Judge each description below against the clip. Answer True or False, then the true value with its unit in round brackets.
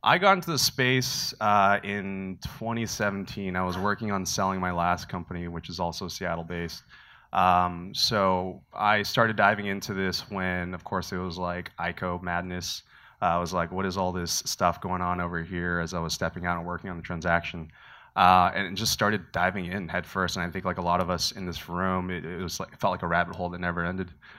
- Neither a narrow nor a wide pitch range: False (1.7 semitones)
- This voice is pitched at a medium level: False (90 Hz)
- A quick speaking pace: True (225 wpm)